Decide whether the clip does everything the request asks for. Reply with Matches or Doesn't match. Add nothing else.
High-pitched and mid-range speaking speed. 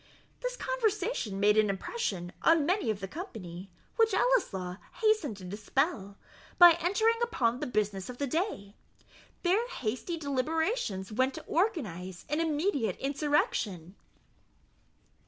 Doesn't match